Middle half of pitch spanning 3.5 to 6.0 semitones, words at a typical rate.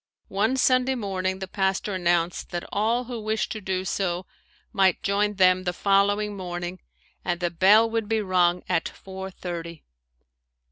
No: average, 2.8 semitones; average, 155 wpm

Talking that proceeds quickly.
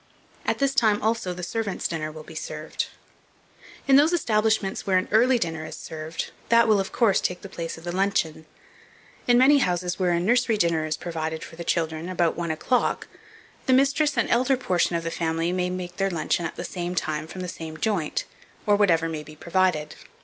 Yes: fast, 210 wpm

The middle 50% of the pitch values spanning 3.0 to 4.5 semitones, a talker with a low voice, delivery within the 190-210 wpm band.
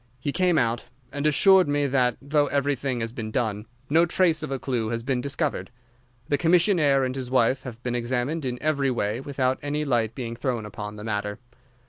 Yes: average, 3.5 semitones; low, 130 Hz; average, 195 wpm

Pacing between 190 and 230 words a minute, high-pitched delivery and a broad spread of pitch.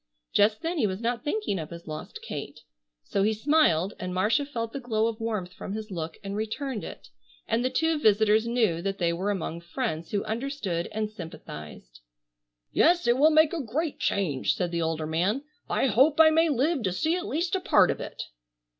Yes: average, 200 wpm; high, 220 Hz; wide, 7.6 semitones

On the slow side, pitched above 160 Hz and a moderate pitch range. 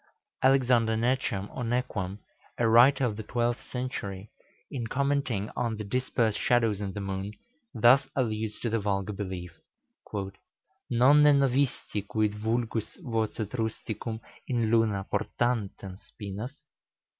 No: slow, 120 wpm; low, 115 Hz; average, 3.3 semitones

